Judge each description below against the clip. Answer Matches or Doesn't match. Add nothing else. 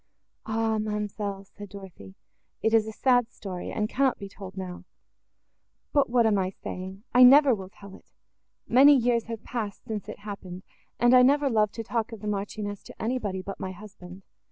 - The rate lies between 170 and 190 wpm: Matches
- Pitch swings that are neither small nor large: Matches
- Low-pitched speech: Doesn't match